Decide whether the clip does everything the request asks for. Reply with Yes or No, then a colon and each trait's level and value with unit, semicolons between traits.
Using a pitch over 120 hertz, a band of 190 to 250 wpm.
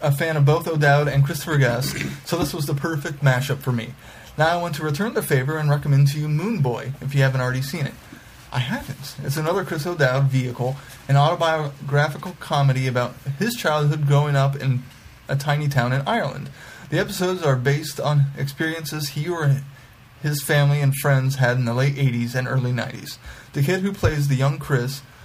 Yes: medium, 140 Hz; average, 195 wpm